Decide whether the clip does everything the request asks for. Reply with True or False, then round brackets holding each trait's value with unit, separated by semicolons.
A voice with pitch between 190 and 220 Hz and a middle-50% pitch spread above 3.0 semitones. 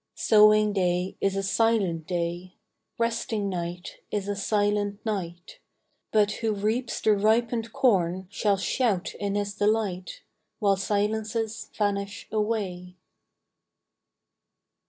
False (205 Hz; 2.5 semitones)